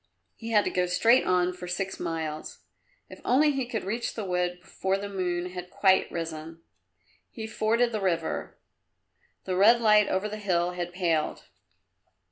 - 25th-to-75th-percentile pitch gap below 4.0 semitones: Yes, average, 3.4 semitones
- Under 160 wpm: No, average, 165 wpm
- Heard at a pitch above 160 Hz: Yes, medium, 185 Hz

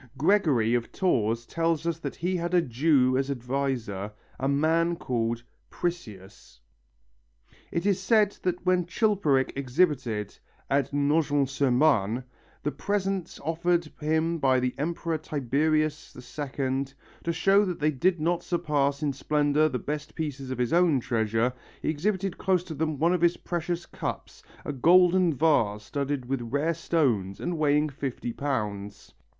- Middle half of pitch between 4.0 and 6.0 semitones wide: Yes, average, 4.7 semitones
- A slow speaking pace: No, average, 150 wpm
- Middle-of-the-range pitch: Yes, medium, 150 Hz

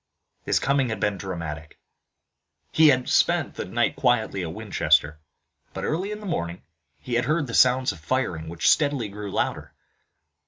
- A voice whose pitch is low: Yes, low, 110 Hz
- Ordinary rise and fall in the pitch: No, wide, 7.8 semitones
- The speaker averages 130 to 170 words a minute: Yes, average, 165 wpm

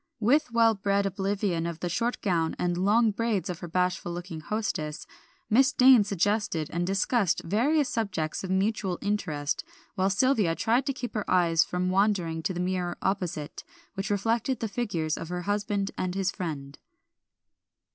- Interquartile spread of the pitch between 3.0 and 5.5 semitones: Yes, average, 3.9 semitones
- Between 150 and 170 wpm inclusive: Yes, average, 165 wpm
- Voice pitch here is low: No, high, 195 Hz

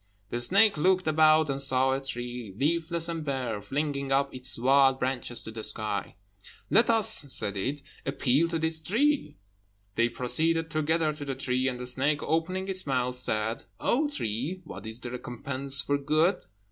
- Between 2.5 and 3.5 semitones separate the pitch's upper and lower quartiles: No, average, 4.3 semitones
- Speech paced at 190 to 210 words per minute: No, average, 170 wpm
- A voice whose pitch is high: No, medium, 140 Hz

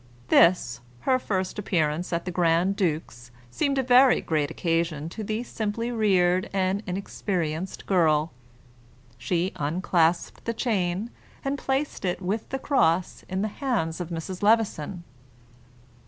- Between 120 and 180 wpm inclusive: Yes, slow, 135 wpm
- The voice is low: No, medium, 185 Hz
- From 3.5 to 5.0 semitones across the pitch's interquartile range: Yes, average, 4.7 semitones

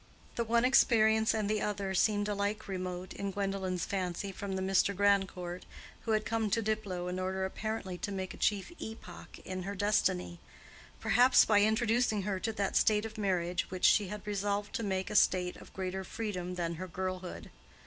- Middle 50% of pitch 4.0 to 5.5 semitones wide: No, narrow, 2.5 semitones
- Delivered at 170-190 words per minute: Yes, average, 180 wpm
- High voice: Yes, high, 200 Hz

